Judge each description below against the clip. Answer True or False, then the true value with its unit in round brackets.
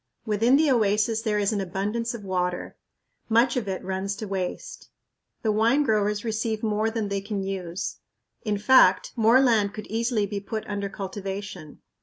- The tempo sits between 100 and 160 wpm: False (170 wpm)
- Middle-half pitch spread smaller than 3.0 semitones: True (2.4 semitones)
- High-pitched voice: True (210 Hz)